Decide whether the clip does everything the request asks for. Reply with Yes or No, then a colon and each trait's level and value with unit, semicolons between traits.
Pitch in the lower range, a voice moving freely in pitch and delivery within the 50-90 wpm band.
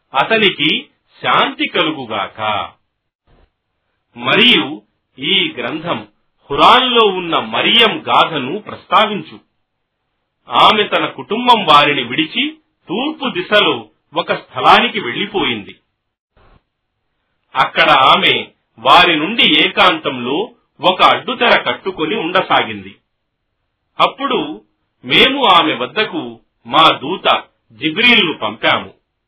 No: high, 210 Hz; wide, 7.9 semitones; average, 80 wpm